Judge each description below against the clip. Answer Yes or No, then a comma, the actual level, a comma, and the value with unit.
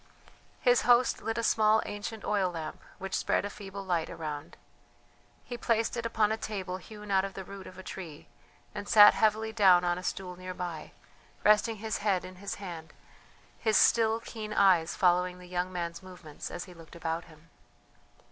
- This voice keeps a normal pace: Yes, average, 185 wpm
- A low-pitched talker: No, high, 195 Hz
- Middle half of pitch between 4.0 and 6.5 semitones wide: No, average, 3.3 semitones